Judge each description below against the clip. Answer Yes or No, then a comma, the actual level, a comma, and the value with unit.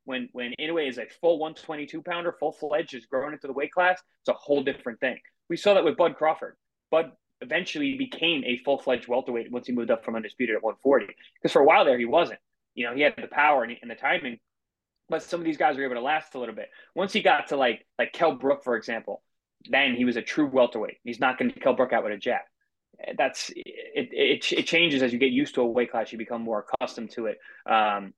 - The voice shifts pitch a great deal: Yes, wide, 5.7 semitones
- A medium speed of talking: No, fast, 255 wpm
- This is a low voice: No, medium, 150 Hz